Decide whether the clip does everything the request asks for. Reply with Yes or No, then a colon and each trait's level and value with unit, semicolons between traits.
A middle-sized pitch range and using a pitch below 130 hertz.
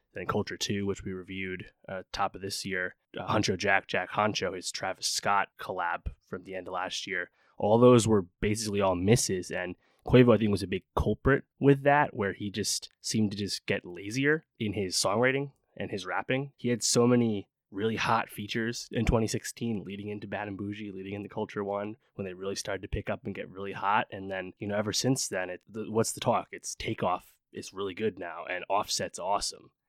Yes: average, 3.0 semitones; low, 105 Hz